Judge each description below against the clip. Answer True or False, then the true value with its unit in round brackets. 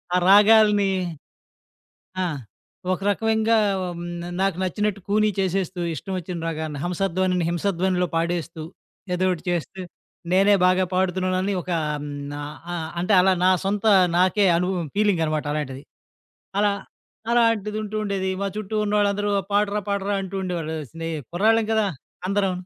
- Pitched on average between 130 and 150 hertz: False (190 Hz)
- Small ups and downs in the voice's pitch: False (3.0 semitones)